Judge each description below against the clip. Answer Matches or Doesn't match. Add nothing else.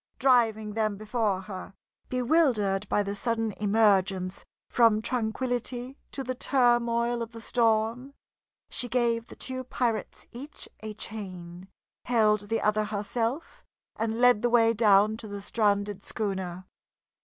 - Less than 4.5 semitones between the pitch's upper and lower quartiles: Matches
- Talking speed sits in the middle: Doesn't match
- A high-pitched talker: Matches